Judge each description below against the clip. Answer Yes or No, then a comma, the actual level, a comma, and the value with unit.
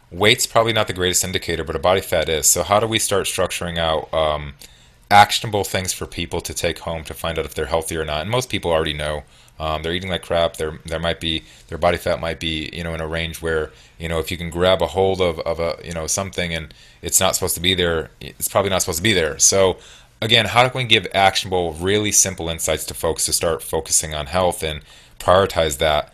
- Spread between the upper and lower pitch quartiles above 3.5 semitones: No, average, 3.0 semitones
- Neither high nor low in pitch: No, very low, 85 Hz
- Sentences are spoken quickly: Yes, fast, 245 wpm